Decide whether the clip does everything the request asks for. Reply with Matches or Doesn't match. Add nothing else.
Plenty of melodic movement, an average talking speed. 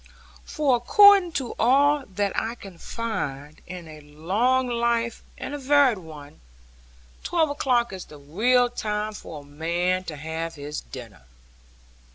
Matches